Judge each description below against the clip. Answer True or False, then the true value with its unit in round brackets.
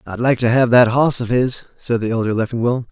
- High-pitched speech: False (120 Hz)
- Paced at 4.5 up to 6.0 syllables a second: True (5.6 syllables/s)